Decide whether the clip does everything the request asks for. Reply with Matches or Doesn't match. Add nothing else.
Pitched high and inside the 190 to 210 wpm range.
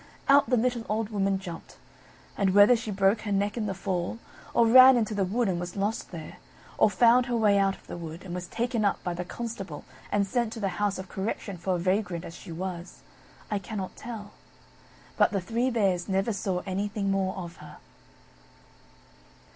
Matches